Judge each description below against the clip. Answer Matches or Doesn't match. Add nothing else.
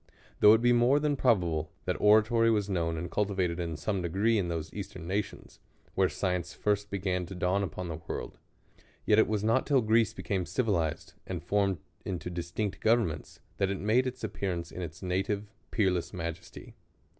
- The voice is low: Matches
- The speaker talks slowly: Doesn't match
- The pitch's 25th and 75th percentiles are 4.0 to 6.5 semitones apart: Doesn't match